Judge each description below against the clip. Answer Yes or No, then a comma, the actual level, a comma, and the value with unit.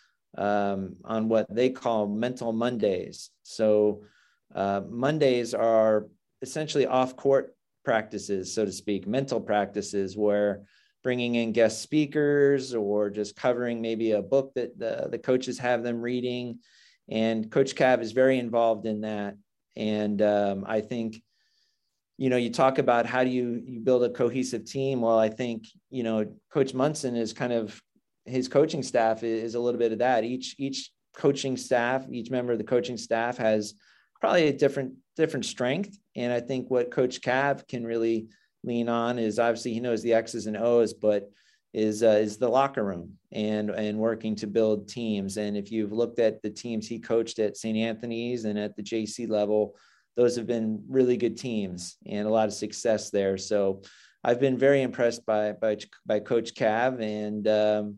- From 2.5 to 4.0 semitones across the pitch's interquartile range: Yes, average, 2.8 semitones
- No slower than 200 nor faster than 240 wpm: No, average, 175 wpm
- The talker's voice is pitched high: No, low, 115 Hz